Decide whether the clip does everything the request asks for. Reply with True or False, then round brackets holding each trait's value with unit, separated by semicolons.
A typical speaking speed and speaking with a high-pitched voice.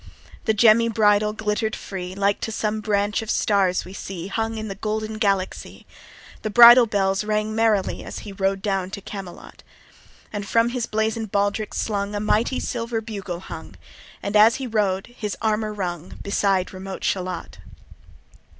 True (160 wpm; 210 Hz)